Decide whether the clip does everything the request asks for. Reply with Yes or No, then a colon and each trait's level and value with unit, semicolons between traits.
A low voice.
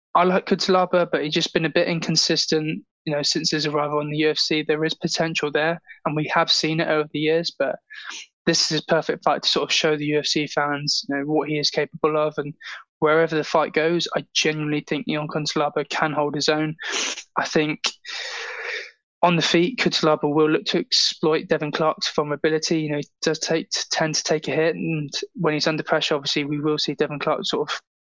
No: medium, 155 Hz